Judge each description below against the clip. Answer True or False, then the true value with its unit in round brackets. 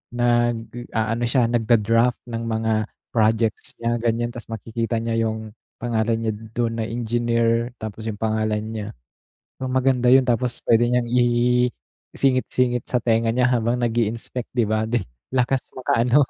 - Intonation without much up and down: True (1.5 semitones)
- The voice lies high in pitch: False (115 Hz)